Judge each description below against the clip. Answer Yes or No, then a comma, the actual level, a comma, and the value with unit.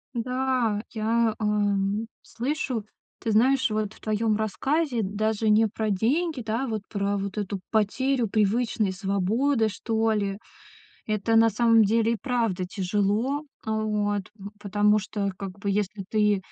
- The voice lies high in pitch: Yes, high, 215 Hz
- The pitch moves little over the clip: Yes, narrow, 2.1 semitones